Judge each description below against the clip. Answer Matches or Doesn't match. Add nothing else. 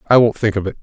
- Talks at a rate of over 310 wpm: Matches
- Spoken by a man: Matches